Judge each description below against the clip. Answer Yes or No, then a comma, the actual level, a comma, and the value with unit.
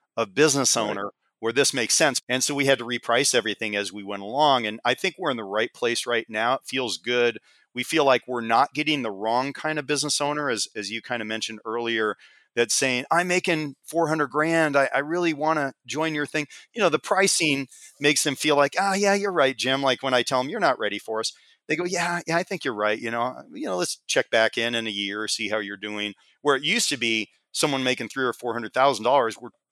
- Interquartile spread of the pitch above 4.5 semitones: Yes, average, 4.9 semitones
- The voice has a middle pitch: No, low, 130 Hz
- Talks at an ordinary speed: No, fast, 255 wpm